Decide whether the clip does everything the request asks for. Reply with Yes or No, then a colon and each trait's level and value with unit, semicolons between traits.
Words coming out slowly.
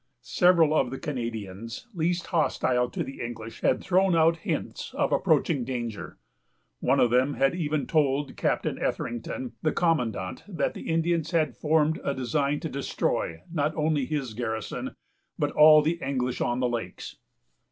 No: average, 160 wpm